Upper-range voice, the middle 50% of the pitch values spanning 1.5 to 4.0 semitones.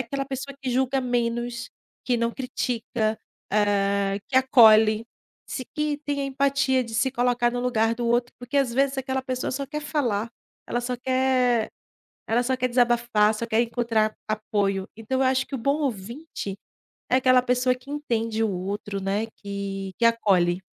Yes: high, 240 Hz; average, 3.2 semitones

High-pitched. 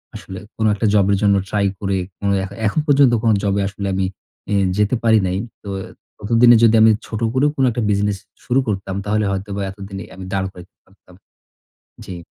No: low, 100 Hz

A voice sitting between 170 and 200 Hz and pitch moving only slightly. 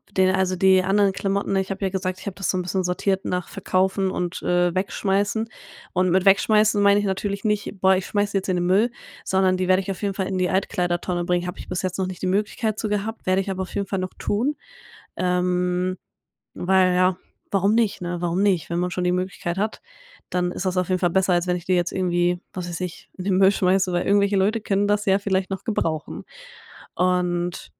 Yes: medium, 185 Hz; narrow, 1.6 semitones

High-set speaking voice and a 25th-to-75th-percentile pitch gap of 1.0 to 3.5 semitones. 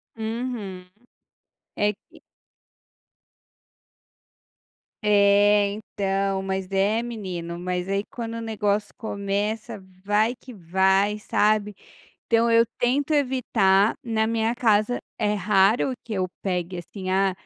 Yes: high, 205 Hz; average, 2.7 semitones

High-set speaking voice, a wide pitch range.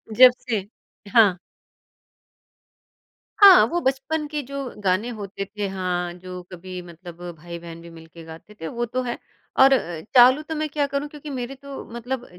Yes: high, 230 Hz; wide, 7.4 semitones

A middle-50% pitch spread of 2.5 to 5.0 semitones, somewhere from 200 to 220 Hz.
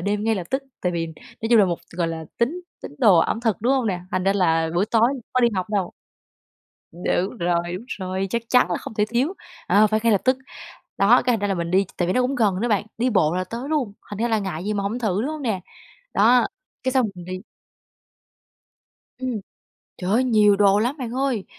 Yes: average, 4.5 semitones; high, 210 Hz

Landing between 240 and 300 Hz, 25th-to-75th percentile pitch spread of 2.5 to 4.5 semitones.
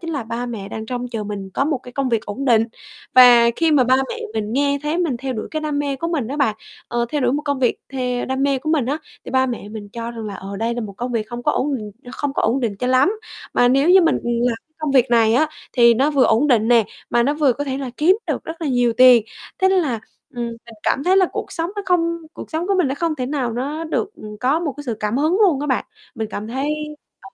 Yes: very high, 255 Hz; average, 4.0 semitones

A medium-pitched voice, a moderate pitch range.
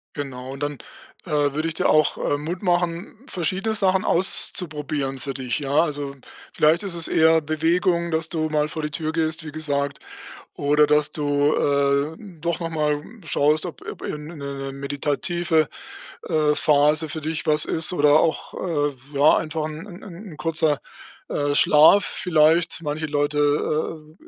No: medium, 155 Hz; narrow, 2.1 semitones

